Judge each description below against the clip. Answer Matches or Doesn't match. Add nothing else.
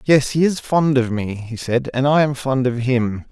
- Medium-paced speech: Doesn't match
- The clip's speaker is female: Doesn't match